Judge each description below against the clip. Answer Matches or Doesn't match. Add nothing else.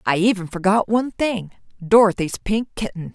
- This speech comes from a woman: Matches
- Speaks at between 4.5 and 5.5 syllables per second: Matches